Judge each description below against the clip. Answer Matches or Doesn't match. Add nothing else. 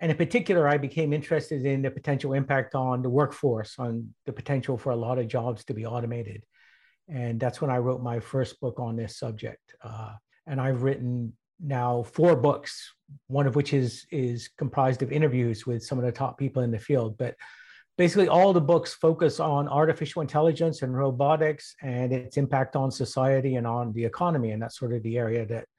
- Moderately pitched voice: Doesn't match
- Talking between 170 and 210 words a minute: Matches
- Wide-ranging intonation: Doesn't match